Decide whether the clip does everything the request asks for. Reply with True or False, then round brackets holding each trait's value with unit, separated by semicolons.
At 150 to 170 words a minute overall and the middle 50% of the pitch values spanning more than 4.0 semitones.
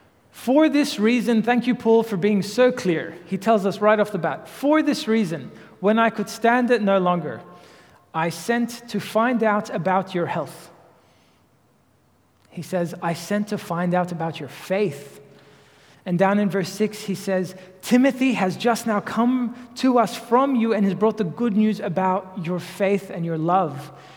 False (180 wpm; 4.4 semitones)